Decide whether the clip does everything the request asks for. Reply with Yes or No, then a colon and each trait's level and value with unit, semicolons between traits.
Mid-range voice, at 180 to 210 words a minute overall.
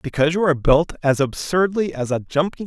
Yes: medium, 160 Hz; fast, 205 wpm